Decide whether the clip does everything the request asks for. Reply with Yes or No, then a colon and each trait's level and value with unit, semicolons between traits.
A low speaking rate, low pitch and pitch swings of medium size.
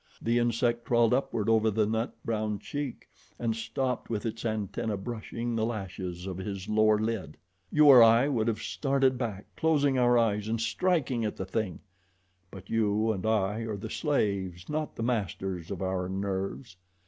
No: average, 170 wpm; low, 110 Hz; average, 3.1 semitones